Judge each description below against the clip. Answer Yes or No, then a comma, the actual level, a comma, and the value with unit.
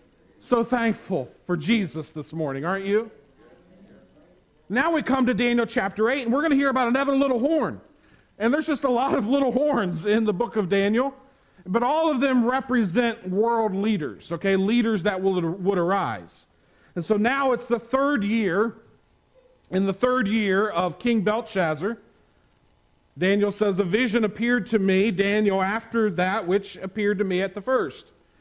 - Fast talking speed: No, average, 170 wpm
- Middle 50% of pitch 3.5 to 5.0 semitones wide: Yes, average, 4.4 semitones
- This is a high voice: Yes, high, 215 Hz